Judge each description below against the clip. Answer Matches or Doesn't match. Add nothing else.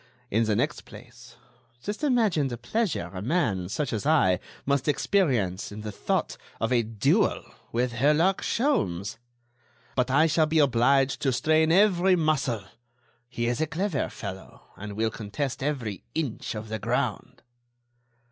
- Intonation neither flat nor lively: Doesn't match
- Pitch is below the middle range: Matches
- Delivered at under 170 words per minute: Matches